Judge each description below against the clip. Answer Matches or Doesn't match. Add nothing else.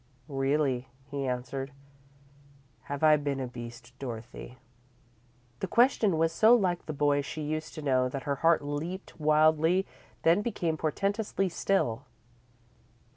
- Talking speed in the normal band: Doesn't match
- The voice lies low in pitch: Doesn't match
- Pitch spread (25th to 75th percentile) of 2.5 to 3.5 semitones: Doesn't match